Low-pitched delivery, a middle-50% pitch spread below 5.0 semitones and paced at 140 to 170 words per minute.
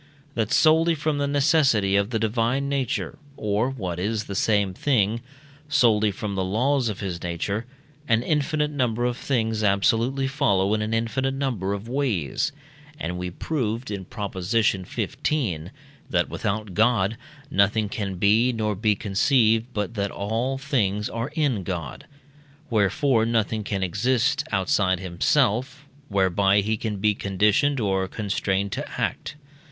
Yes: low, 110 Hz; average, 4.5 semitones; average, 145 wpm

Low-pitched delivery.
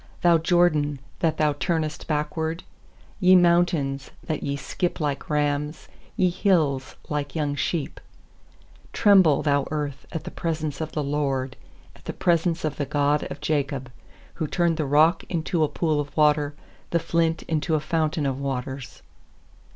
No: medium, 150 Hz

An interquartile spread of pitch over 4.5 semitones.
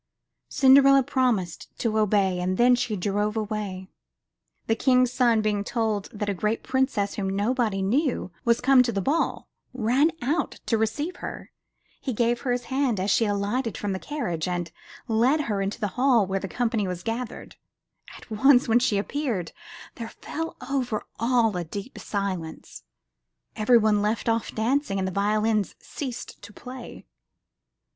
No: average, 3.8 semitones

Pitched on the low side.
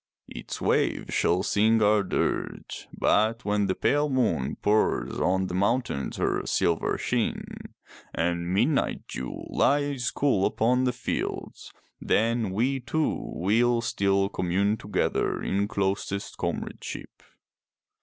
Yes: low, 105 Hz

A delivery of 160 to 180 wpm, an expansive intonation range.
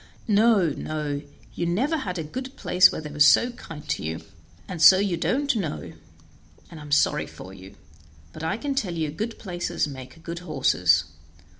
Yes: average, 175 wpm; wide, 5.8 semitones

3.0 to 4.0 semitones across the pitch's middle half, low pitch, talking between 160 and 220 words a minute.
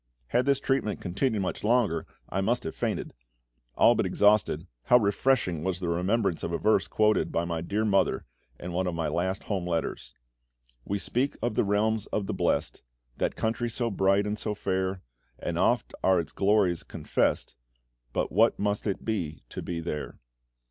Yes: average, 3.7 semitones; low, 100 Hz; average, 180 wpm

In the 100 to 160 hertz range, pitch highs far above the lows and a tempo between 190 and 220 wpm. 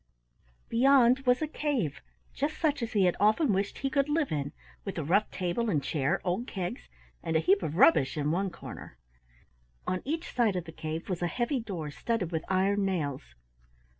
No: high, 190 Hz; wide, 6.8 semitones; average, 195 wpm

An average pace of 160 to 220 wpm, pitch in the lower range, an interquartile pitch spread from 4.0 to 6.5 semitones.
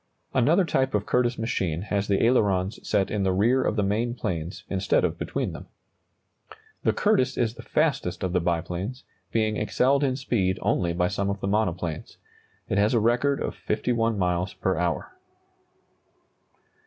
Yes: average, 165 wpm; low, 105 Hz; average, 4.6 semitones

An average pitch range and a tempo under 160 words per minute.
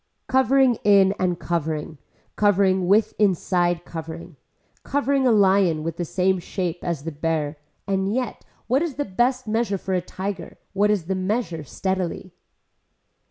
Yes: average, 3.7 semitones; average, 150 wpm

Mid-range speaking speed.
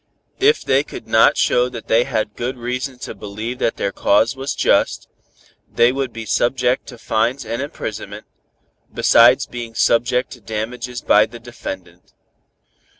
Yes: average, 150 wpm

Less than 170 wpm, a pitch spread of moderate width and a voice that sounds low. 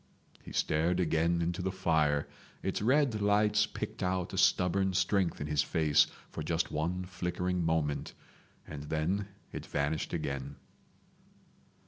Yes: slow, 135 wpm; average, 3.3 semitones; very low, 85 Hz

